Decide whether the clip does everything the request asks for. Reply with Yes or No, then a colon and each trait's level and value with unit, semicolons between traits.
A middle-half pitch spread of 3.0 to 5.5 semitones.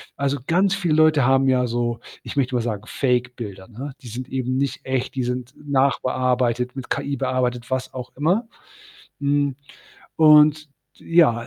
No: narrow, 2.6 semitones